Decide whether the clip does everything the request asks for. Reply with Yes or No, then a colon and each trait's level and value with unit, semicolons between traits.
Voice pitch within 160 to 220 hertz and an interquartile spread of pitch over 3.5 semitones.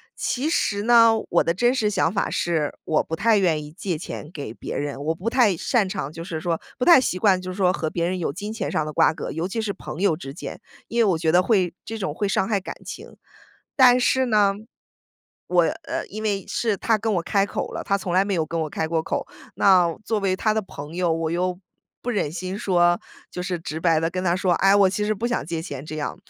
Yes: medium, 185 Hz; average, 4.1 semitones